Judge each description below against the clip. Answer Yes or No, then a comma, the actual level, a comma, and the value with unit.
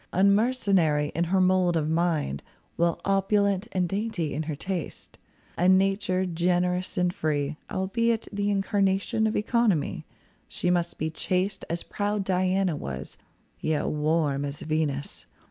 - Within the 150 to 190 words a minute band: No, slow, 135 wpm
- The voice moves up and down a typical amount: Yes, average, 3.7 semitones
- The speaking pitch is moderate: Yes, medium, 180 Hz